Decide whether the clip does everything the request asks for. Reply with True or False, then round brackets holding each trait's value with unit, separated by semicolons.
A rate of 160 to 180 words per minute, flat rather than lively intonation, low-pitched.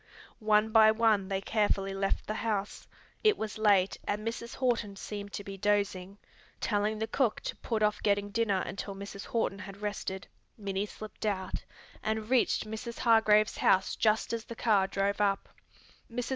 False (170 wpm; 1.8 semitones; 210 Hz)